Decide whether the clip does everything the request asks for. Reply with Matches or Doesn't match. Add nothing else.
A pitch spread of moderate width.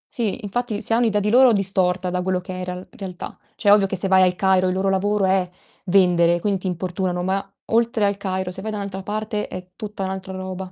Doesn't match